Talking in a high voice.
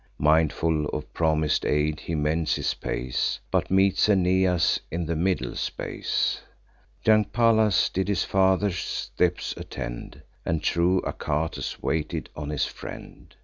No: very low, 85 Hz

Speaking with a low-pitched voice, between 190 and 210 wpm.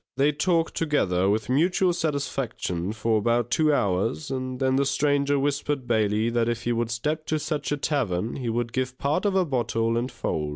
Yes: low, 130 Hz; average, 195 wpm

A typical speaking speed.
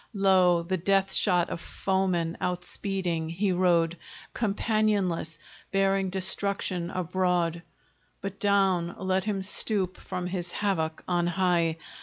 No: slow, 115 wpm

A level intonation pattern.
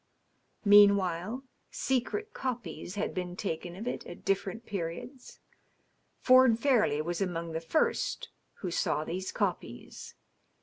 No: wide, 5.5 semitones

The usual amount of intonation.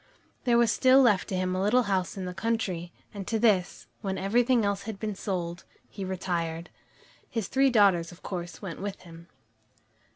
Yes: average, 3.6 semitones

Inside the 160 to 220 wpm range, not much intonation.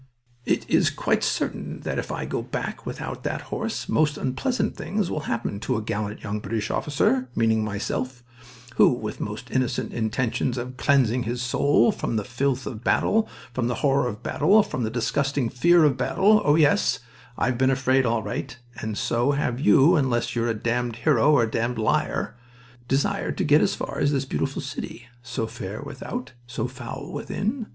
No: average, 185 wpm; average, 3.4 semitones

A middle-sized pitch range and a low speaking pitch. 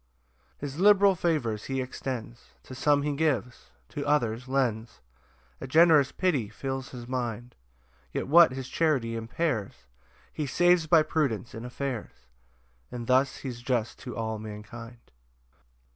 Yes: average, 4.2 semitones; low, 130 Hz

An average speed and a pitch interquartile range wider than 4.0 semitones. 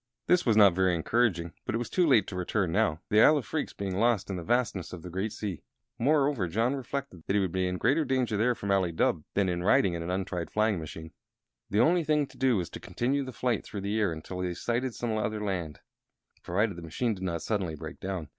No: fast, 245 wpm; average, 5.1 semitones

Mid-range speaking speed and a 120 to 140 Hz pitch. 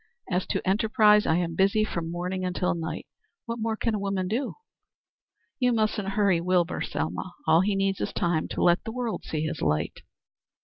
No: average, 185 wpm; high, 190 Hz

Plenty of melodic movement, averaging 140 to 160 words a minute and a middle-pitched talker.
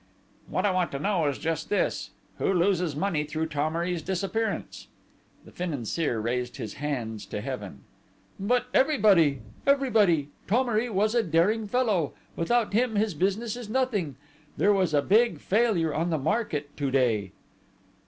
Yes: wide, 6.7 semitones; average, 150 wpm; medium, 180 Hz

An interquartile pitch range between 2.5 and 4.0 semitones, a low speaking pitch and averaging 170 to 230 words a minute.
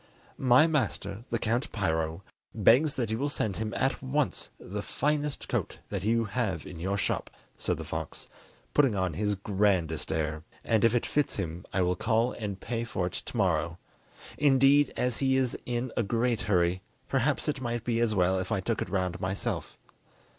No: average, 5.1 semitones; low, 110 Hz; average, 190 wpm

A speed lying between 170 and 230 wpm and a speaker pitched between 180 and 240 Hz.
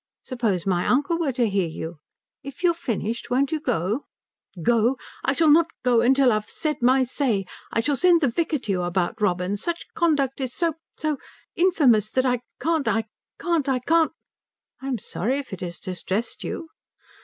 No: average, 190 wpm; very high, 255 Hz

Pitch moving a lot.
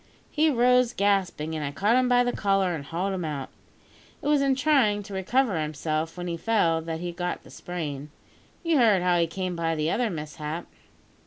Yes: wide, 6.2 semitones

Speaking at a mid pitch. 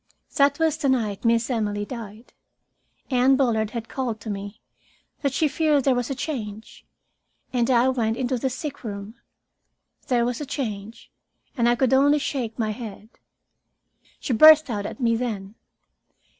No: high, 240 Hz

